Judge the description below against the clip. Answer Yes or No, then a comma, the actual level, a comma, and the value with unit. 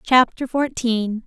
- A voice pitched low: No, high, 240 Hz